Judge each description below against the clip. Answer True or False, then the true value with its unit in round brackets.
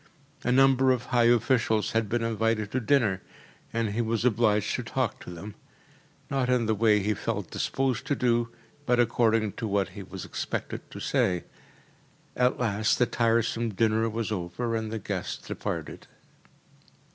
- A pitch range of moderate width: False (2.3 semitones)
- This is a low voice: True (115 Hz)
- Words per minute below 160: False (165 wpm)